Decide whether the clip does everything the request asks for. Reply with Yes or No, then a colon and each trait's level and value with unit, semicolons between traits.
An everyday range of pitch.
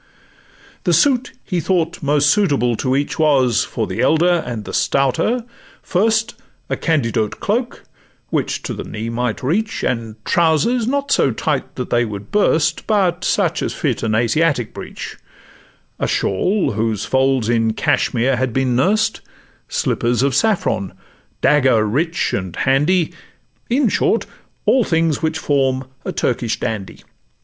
No: wide, 6.9 semitones